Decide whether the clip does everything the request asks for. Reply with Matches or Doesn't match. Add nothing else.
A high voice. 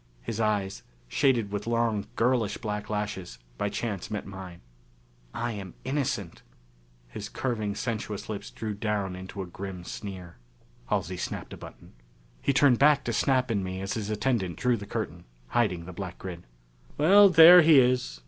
Doesn't match